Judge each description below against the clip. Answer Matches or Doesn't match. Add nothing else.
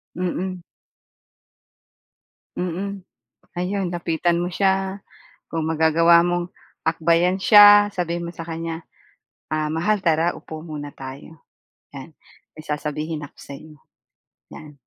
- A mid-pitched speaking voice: Matches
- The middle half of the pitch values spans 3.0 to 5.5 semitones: Doesn't match